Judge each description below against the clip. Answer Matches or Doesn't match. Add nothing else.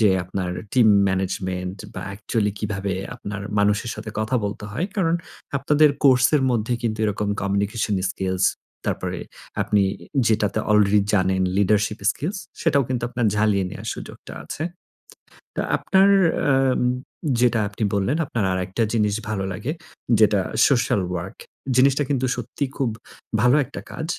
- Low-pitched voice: Matches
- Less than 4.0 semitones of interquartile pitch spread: Doesn't match